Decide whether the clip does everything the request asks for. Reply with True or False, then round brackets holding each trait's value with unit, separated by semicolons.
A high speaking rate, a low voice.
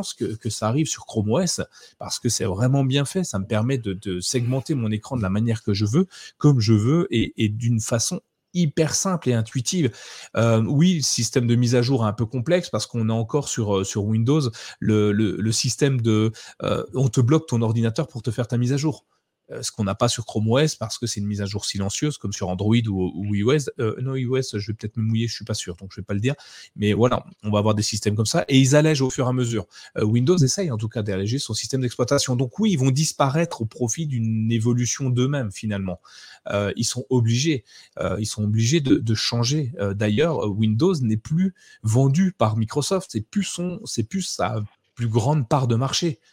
True (240 wpm; 120 Hz)